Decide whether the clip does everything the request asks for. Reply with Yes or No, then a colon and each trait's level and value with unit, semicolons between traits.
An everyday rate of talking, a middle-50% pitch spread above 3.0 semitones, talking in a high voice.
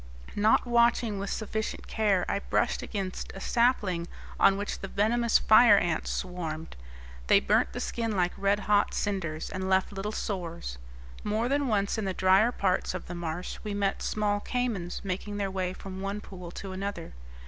No: average, 175 wpm; narrow, 2.5 semitones; high, 200 Hz